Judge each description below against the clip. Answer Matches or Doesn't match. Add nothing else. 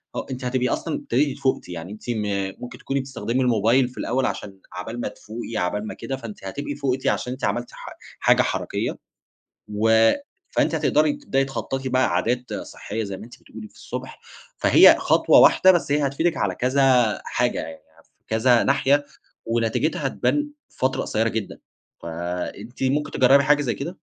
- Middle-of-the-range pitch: Doesn't match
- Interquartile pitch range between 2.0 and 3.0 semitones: Doesn't match